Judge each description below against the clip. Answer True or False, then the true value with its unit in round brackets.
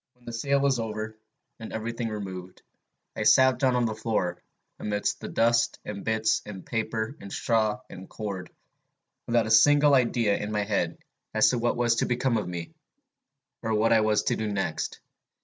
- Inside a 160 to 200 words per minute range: True (185 wpm)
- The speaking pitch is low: True (110 Hz)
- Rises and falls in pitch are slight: True (2.3 semitones)